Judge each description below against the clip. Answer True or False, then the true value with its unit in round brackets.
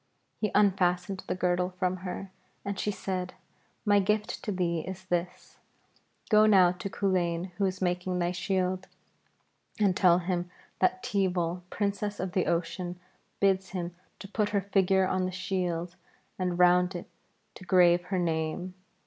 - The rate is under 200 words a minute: True (155 wpm)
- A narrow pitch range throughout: True (1.5 semitones)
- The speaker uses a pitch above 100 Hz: True (185 Hz)